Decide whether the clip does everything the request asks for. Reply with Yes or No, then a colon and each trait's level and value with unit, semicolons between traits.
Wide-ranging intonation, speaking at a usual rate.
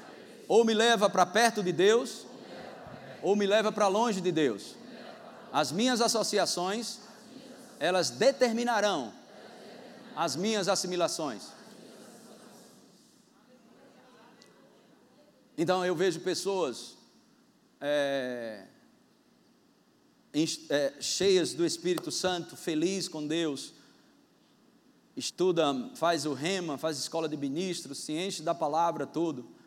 No: wide, 5.8 semitones; slow, 95 wpm